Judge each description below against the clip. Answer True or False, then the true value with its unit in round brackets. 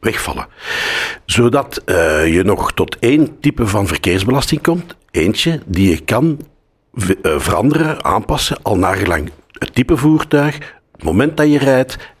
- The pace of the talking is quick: False (140 wpm)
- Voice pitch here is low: True (130 Hz)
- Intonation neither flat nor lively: False (7.7 semitones)